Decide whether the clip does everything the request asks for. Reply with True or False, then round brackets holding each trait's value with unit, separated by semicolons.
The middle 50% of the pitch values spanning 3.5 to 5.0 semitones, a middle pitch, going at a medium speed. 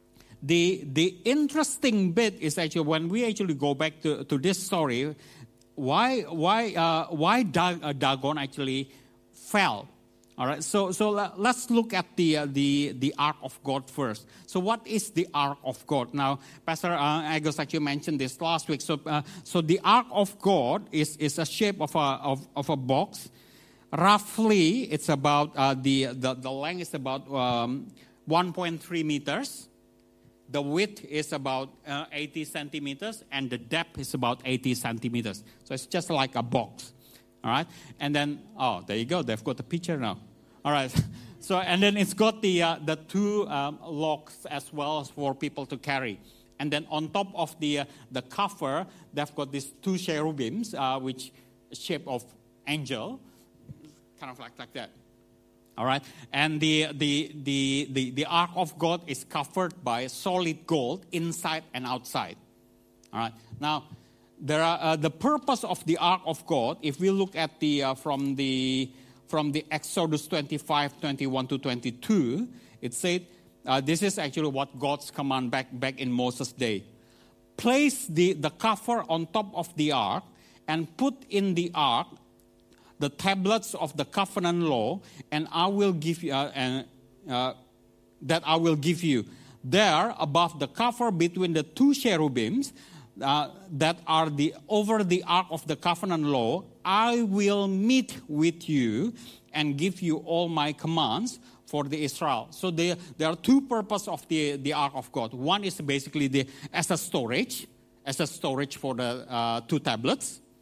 True (4.7 semitones; 150 Hz; 170 wpm)